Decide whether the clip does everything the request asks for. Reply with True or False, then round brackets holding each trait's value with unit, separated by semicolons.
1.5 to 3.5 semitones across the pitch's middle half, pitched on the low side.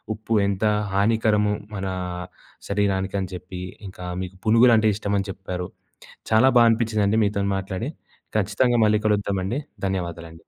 True (2.4 semitones; 100 Hz)